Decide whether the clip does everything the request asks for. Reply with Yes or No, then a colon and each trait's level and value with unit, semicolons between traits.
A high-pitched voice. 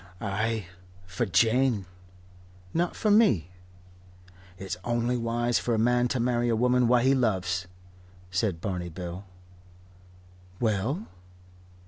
No: low, 115 Hz